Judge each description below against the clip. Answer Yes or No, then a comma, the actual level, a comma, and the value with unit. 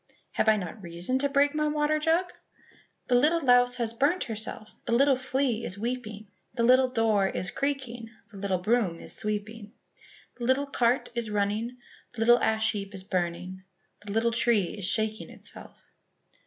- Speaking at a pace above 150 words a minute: Yes, average, 170 wpm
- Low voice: No, high, 230 Hz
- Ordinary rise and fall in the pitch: Yes, average, 3.8 semitones